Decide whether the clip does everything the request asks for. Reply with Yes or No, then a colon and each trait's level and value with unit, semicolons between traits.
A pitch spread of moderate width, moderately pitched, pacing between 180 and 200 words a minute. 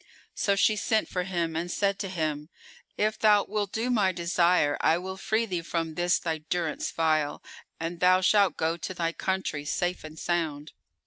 Yes: average, 3.1 semitones; medium, 175 Hz; average, 185 wpm